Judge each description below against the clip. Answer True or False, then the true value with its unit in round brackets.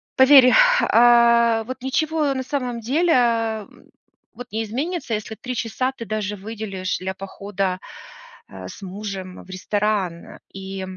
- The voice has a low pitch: False (225 Hz)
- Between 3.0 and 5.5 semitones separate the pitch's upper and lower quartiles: True (4.4 semitones)